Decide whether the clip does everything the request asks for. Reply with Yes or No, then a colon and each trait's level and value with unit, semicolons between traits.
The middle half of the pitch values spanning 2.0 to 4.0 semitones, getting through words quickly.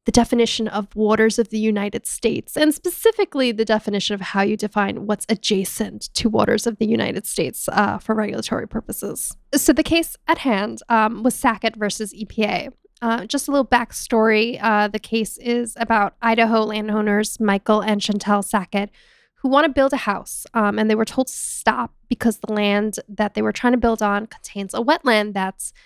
No: narrow, 2.4 semitones; average, 190 wpm